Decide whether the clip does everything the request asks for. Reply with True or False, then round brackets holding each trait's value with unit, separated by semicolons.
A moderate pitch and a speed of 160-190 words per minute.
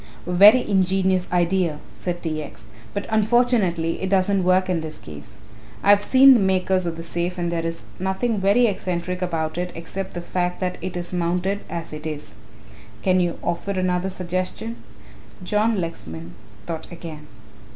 True (180 Hz; 170 wpm)